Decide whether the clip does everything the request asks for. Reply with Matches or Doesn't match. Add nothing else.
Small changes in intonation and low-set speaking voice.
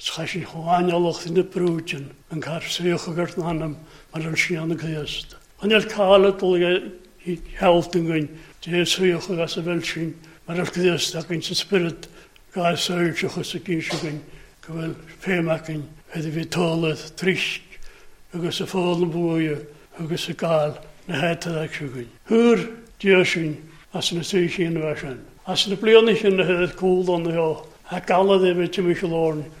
Doesn't match